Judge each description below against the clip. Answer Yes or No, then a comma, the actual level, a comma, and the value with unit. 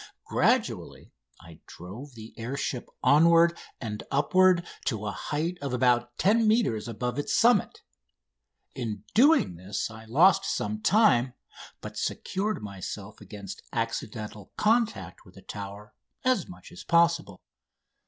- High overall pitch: No, low, 125 Hz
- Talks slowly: Yes, slow, 130 wpm